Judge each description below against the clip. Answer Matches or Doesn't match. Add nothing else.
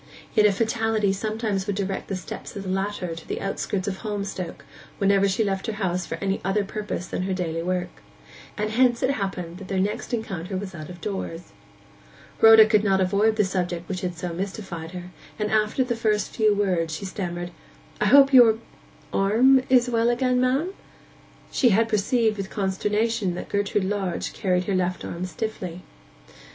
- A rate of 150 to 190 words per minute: Matches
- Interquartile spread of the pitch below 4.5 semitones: Matches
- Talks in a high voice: Matches